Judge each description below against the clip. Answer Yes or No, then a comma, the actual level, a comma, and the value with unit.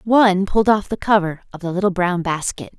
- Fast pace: Yes, fast, 215 wpm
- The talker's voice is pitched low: No, high, 190 Hz